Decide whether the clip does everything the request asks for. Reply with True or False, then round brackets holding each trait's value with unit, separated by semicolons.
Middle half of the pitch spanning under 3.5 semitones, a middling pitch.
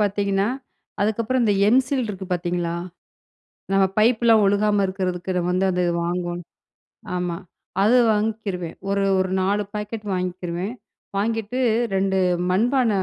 False (3.1 semitones; 200 Hz)